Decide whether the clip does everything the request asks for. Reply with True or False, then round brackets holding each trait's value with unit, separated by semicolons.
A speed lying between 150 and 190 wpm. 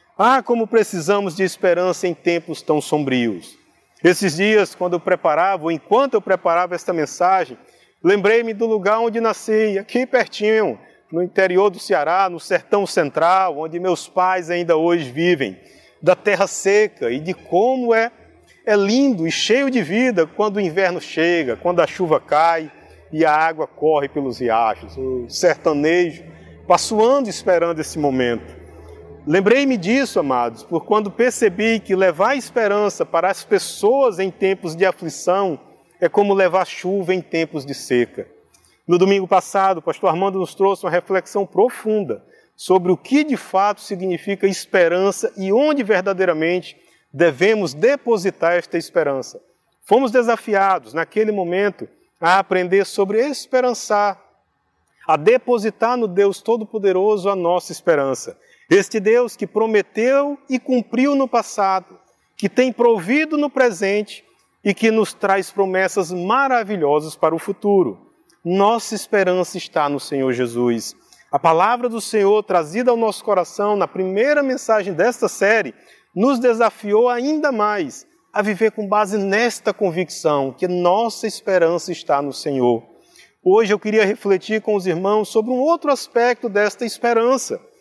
False (140 wpm)